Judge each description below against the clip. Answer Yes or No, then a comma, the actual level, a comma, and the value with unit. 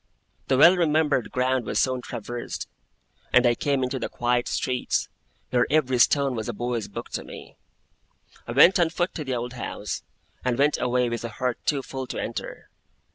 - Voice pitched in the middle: No, low, 130 Hz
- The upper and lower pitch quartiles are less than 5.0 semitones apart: Yes, narrow, 2.6 semitones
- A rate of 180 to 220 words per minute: Yes, average, 185 wpm